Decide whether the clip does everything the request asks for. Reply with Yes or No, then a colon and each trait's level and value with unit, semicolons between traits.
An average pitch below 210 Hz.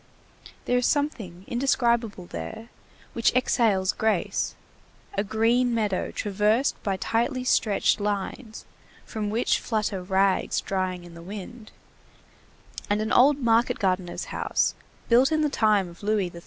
No: high, 215 Hz